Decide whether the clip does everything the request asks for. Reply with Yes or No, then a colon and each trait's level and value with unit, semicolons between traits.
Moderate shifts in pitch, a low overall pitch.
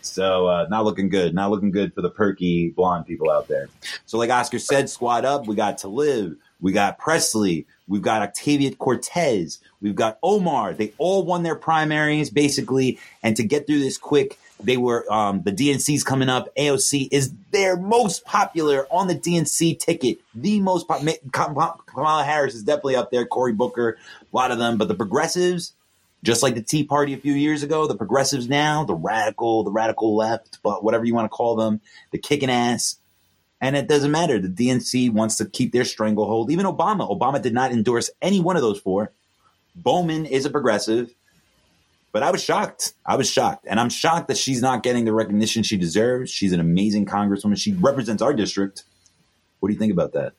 No: wide, 5.7 semitones; low, 125 Hz